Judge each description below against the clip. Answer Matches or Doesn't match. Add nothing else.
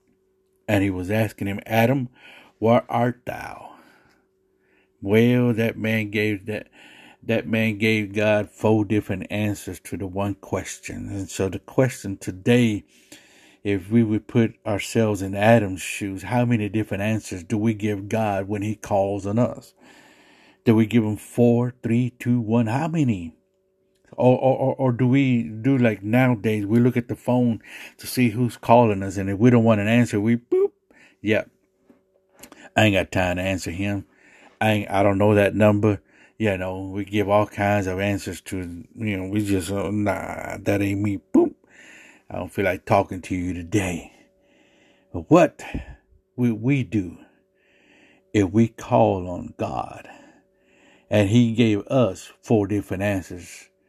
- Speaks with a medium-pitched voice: Doesn't match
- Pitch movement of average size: Matches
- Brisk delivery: Doesn't match